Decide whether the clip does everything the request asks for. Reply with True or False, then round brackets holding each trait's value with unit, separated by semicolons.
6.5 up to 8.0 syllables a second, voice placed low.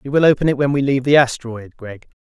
True (7.0 syllables/s; 130 Hz)